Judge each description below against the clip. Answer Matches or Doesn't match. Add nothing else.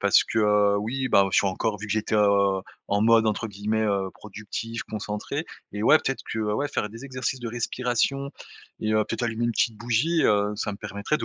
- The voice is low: Matches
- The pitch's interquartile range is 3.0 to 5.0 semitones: Doesn't match